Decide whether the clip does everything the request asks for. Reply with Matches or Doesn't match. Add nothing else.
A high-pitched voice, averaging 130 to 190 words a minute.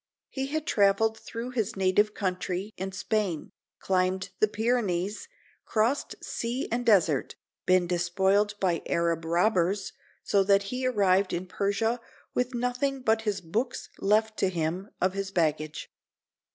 Matches